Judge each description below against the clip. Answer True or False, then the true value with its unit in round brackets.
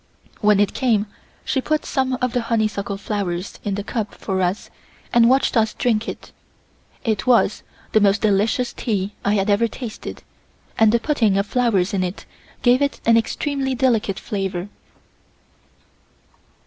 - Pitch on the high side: True (215 Hz)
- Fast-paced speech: False (155 wpm)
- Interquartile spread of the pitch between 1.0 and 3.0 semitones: False (3.4 semitones)